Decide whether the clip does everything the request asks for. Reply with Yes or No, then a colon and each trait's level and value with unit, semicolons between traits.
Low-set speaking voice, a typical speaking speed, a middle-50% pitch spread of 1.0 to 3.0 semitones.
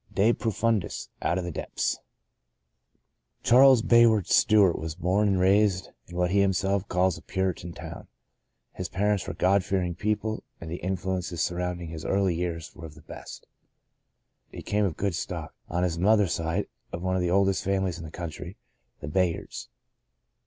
Yes: very low, 95 Hz; average, 175 wpm; narrow, 2.5 semitones